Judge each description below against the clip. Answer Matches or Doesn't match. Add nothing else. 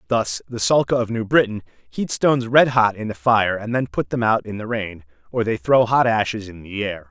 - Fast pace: Matches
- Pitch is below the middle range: Matches